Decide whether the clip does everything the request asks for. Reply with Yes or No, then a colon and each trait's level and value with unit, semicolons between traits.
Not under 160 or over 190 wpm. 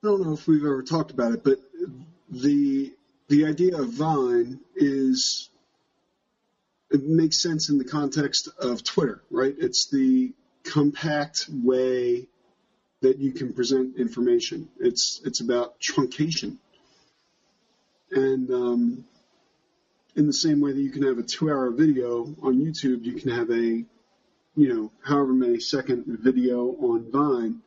No: average, 145 wpm